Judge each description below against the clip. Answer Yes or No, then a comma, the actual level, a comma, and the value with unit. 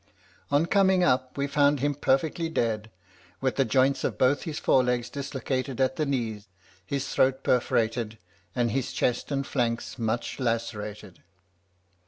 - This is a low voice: Yes, low, 130 Hz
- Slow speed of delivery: No, average, 145 wpm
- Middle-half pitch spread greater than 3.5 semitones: No, average, 3.1 semitones